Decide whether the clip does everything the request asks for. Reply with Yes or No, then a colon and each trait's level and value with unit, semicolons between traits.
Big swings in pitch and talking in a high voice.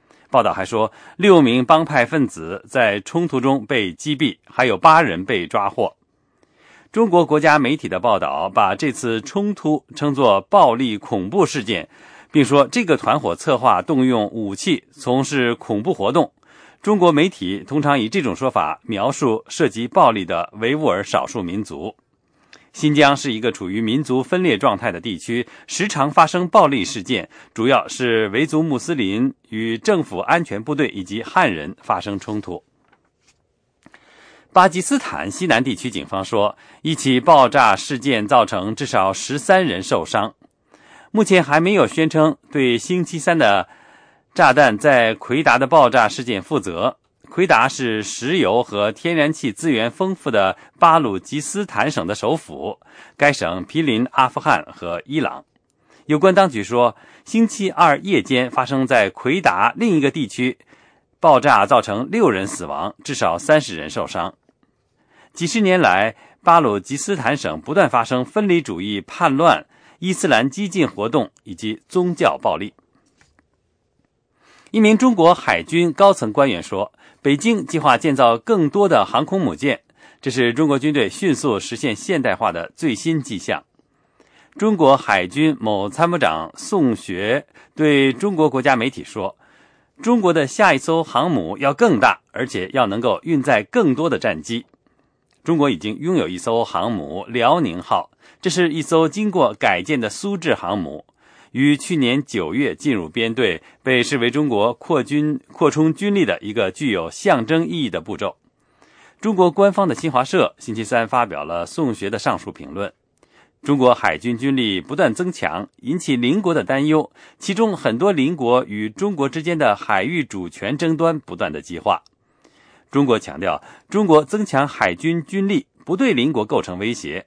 No: wide, 6.3 semitones; medium, 150 Hz